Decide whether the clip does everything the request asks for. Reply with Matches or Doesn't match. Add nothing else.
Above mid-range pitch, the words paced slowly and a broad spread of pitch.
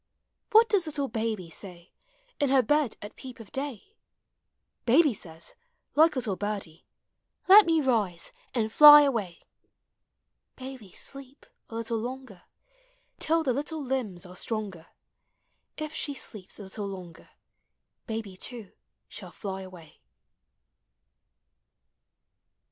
Matches